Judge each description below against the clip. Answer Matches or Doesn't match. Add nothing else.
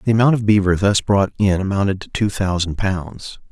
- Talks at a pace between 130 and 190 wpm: Doesn't match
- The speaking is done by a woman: Doesn't match